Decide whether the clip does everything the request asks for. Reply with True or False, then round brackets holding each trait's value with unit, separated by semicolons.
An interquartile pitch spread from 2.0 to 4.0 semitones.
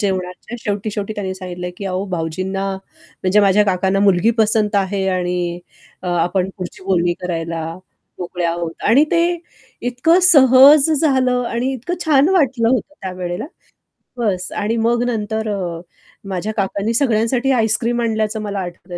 False (4.6 semitones)